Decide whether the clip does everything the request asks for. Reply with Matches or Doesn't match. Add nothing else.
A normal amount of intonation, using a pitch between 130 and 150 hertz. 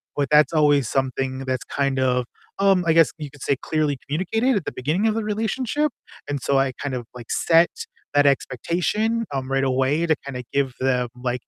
Matches